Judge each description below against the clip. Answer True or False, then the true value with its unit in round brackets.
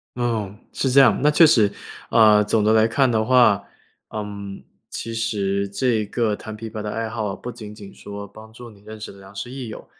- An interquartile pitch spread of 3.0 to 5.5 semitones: False (2.4 semitones)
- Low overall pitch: True (110 Hz)